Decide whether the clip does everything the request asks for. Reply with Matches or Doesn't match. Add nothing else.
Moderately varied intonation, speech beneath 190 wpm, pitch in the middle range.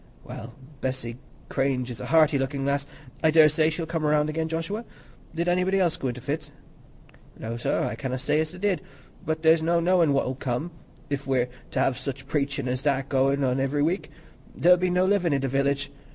Doesn't match